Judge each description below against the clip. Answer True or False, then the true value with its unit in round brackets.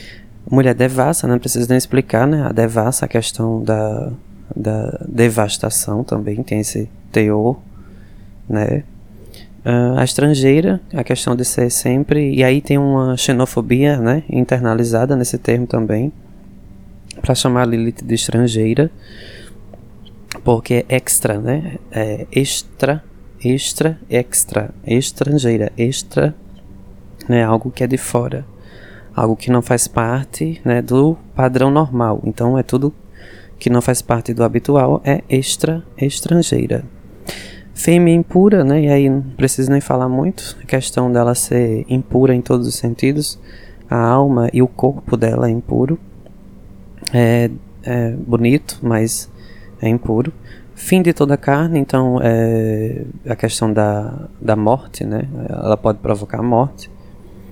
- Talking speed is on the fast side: False (135 wpm)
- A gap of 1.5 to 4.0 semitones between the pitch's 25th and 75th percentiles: True (3.5 semitones)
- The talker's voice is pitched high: False (120 Hz)